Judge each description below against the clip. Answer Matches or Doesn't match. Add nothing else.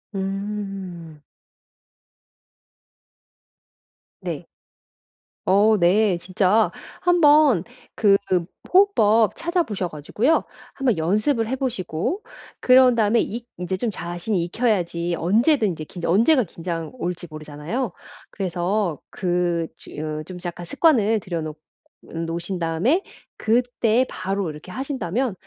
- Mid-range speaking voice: Doesn't match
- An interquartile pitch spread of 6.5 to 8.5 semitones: Doesn't match